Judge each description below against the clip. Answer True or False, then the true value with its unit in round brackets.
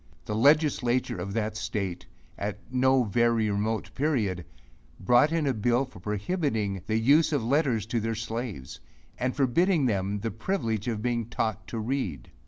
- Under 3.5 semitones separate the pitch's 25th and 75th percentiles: False (3.9 semitones)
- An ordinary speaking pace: True (165 wpm)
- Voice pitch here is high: False (115 Hz)